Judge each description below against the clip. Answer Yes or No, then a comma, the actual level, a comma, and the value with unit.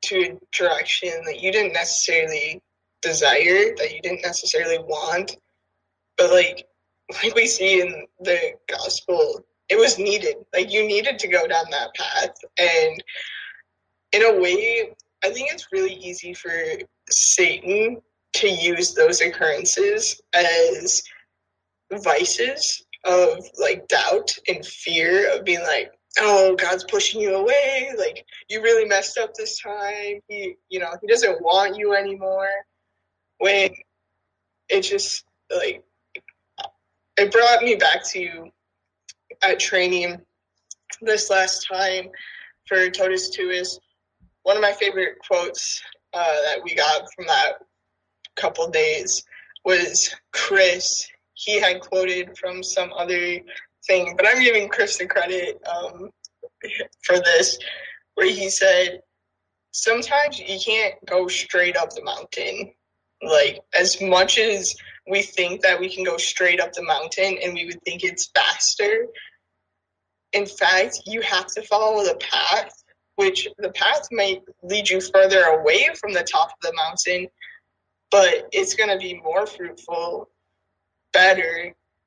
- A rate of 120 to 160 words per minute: Yes, average, 140 wpm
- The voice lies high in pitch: Yes, high, 210 Hz